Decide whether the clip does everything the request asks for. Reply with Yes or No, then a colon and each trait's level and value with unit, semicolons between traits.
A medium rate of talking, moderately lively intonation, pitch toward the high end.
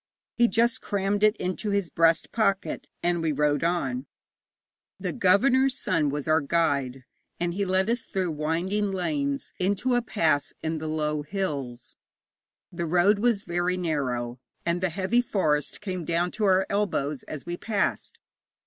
No: average, 160 wpm; average, 4.8 semitones; medium, 175 Hz